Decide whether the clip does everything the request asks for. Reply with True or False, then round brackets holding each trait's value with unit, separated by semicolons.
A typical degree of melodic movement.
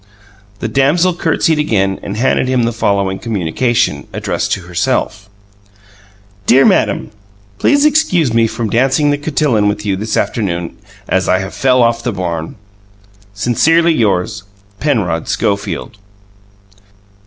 False (5.8 semitones)